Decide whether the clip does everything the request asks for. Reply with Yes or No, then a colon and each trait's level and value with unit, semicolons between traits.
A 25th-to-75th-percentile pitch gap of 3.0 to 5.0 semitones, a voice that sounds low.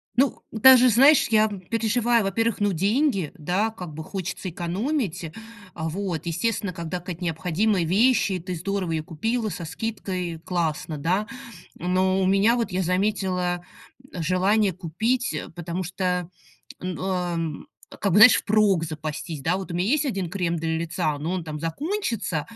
No: average, 4.2 semitones; medium, 185 Hz